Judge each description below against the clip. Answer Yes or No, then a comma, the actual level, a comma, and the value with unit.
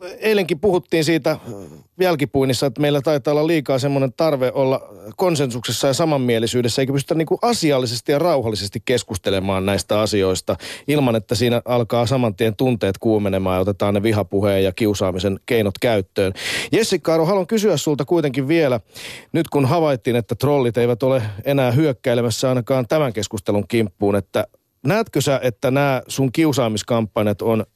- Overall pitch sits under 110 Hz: No, low, 130 Hz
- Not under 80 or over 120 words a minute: No, average, 145 wpm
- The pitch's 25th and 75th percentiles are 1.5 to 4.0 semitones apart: No, average, 5.1 semitones